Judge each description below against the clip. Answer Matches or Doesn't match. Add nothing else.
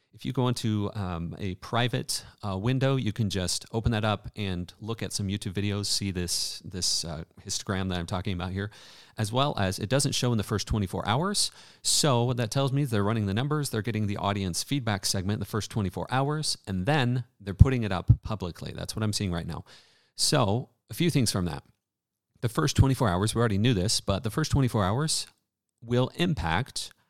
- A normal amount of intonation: Matches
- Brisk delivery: Matches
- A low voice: Matches